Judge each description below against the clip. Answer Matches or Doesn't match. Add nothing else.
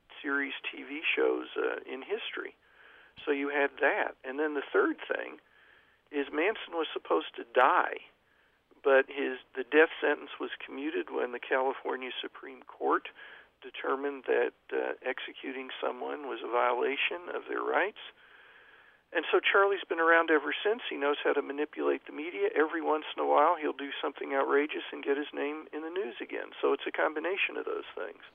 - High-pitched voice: Matches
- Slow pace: Doesn't match